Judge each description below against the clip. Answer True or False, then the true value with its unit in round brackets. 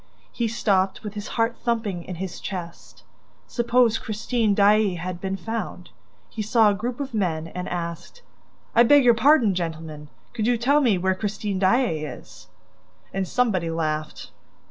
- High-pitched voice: True (205 Hz)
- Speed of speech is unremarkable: True (160 wpm)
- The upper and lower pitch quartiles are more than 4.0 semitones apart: True (4.7 semitones)